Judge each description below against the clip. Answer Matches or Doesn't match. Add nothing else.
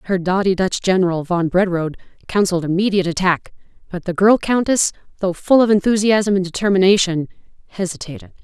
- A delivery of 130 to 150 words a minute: Matches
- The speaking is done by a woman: Matches